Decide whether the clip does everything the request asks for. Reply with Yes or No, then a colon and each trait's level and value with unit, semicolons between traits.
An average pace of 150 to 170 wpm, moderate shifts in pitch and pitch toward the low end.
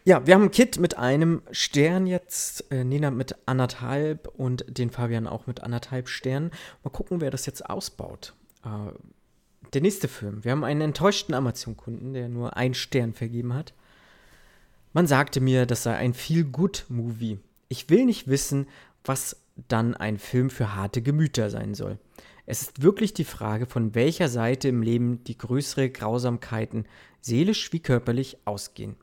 Yes: average, 160 wpm; average, 3.9 semitones; low, 130 Hz